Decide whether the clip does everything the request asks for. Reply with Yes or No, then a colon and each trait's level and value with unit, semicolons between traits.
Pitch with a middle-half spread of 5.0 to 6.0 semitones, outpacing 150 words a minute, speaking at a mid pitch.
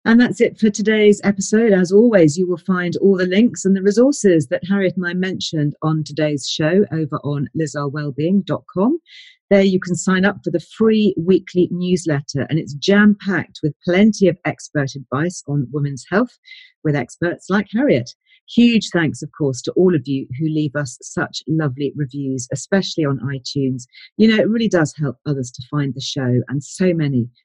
Yes: wide, 5.6 semitones; average, 185 wpm; medium, 170 Hz